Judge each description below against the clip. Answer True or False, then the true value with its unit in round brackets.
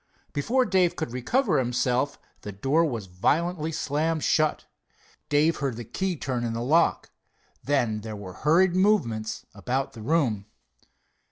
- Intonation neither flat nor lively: False (6.1 semitones)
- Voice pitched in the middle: True (145 Hz)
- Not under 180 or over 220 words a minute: False (145 wpm)